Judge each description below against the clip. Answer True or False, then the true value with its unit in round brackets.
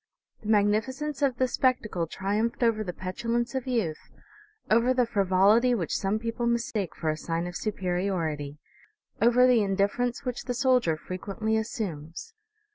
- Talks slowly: False (145 wpm)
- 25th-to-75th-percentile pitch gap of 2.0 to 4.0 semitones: False (4.7 semitones)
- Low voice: False (220 Hz)